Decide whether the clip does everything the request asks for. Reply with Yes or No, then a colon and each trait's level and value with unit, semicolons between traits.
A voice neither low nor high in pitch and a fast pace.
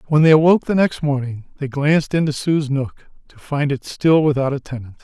Yes: medium, 145 Hz; fast, 215 wpm